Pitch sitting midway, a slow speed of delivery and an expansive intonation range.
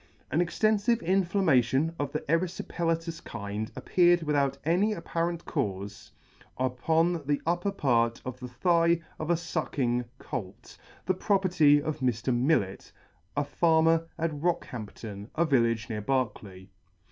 Yes: medium, 150 Hz; slow, 125 wpm; wide, 5.7 semitones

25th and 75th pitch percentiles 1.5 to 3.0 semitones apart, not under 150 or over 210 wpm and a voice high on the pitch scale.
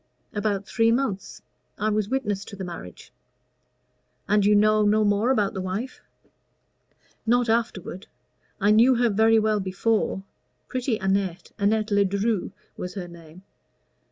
No: narrow, 2.5 semitones; slow, 135 wpm; high, 210 Hz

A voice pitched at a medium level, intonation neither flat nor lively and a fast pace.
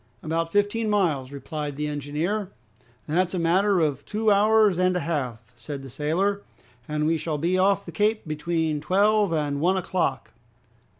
No: medium, 165 Hz; average, 4.9 semitones; average, 165 wpm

